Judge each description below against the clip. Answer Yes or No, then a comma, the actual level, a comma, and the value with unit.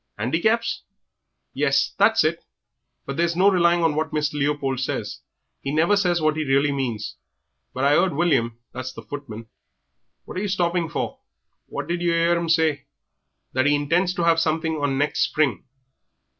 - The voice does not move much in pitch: No, average, 3.7 semitones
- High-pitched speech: No, medium, 155 Hz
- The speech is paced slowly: No, average, 175 wpm